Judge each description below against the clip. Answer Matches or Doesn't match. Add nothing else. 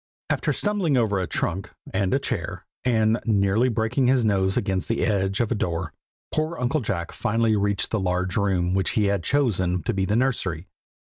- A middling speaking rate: Matches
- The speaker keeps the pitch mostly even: Doesn't match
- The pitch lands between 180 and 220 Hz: Doesn't match